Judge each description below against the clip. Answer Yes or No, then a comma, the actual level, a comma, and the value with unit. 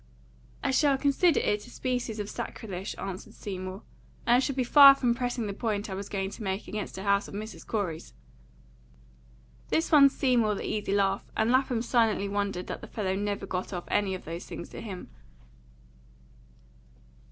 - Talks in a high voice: Yes, high, 210 Hz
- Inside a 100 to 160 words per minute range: No, average, 180 wpm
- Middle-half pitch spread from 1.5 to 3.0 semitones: No, average, 4.0 semitones